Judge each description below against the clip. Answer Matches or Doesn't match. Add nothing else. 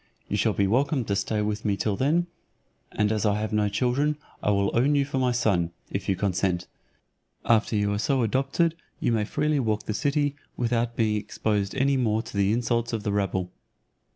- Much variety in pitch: Doesn't match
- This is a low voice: Matches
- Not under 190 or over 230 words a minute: Matches